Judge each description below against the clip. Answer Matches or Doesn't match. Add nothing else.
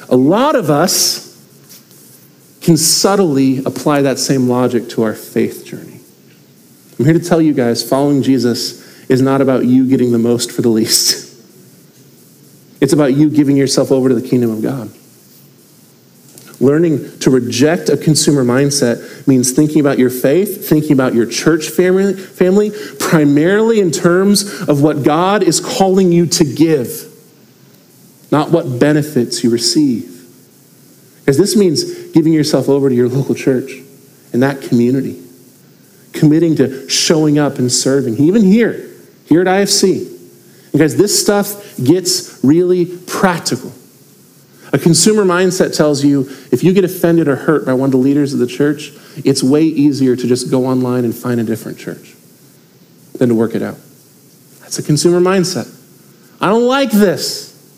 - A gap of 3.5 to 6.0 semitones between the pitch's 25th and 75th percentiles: Matches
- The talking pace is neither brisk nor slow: Matches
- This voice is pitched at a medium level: Matches